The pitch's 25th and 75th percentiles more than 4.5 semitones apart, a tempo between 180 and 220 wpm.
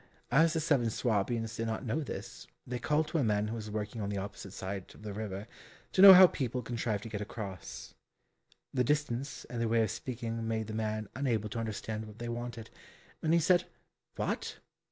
No: average, 3.0 semitones; fast, 205 wpm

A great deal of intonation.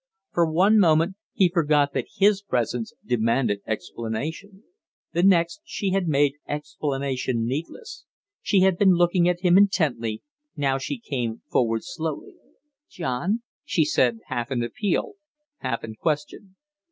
Yes: wide, 7.0 semitones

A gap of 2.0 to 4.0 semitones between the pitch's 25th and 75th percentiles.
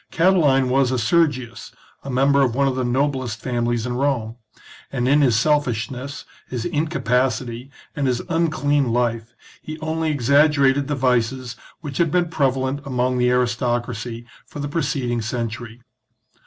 Yes: average, 2.9 semitones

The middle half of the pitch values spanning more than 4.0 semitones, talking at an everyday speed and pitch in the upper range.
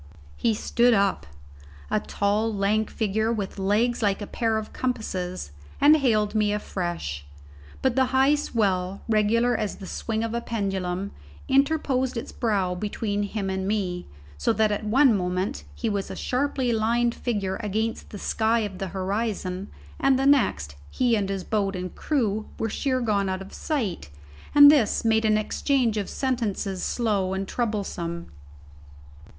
No: average, 3.4 semitones; average, 160 wpm; high, 215 Hz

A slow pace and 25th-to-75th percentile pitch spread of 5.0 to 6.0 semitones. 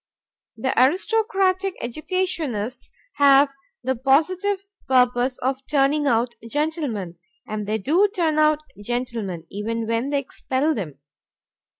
Yes: slow, 110 wpm; average, 5.3 semitones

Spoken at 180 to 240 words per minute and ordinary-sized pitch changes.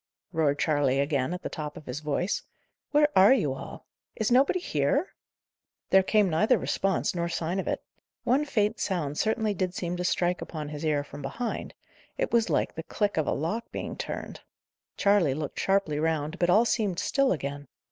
No: average, 190 wpm; wide, 6.0 semitones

